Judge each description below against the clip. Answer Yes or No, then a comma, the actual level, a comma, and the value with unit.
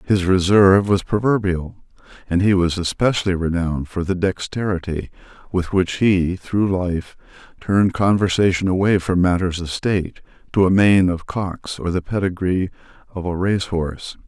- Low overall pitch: Yes, very low, 90 Hz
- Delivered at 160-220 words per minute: No, average, 145 wpm